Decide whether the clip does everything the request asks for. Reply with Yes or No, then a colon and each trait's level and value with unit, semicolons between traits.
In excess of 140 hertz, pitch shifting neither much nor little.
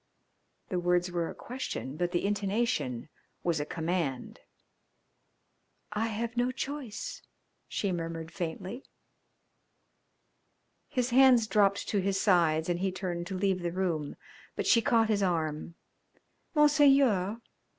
Yes: high, 190 Hz; average, 5.0 semitones